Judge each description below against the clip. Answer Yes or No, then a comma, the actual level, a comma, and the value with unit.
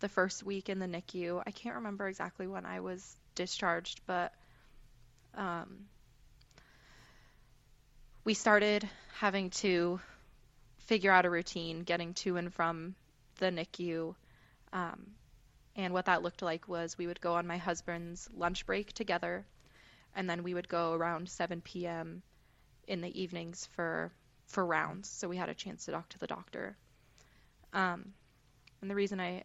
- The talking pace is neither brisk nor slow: Yes, average, 155 wpm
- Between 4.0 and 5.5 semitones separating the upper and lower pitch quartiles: Yes, average, 5.2 semitones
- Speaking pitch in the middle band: Yes, medium, 170 Hz